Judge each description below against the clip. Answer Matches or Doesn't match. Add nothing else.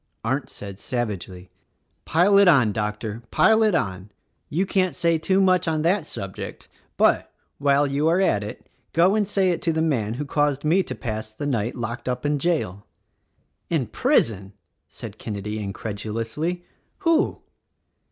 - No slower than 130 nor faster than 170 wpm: Matches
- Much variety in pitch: Matches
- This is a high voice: Doesn't match